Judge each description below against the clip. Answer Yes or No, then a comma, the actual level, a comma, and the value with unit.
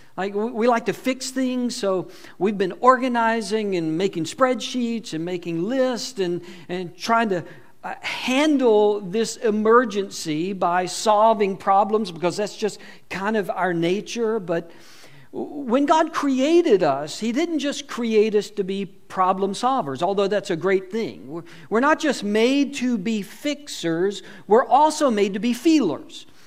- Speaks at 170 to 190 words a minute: No, average, 145 wpm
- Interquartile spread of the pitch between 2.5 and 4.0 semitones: No, average, 5.0 semitones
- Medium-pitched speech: No, high, 210 Hz